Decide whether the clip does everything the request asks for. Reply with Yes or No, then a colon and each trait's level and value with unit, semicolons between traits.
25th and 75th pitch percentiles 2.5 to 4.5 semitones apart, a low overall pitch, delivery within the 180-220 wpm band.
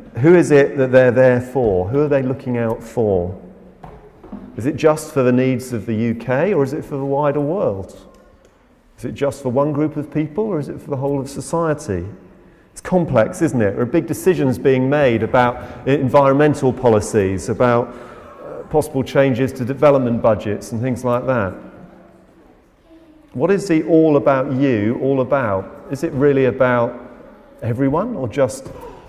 No: average, 3.2 semitones; low, 130 Hz; average, 170 wpm